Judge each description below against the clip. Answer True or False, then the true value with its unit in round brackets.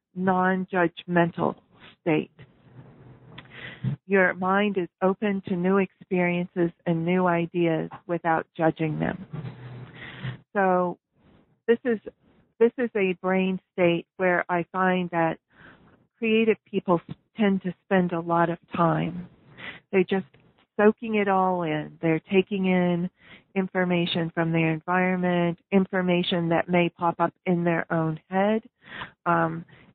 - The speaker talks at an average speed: False (120 wpm)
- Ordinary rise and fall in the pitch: False (2.3 semitones)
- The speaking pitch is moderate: True (175 Hz)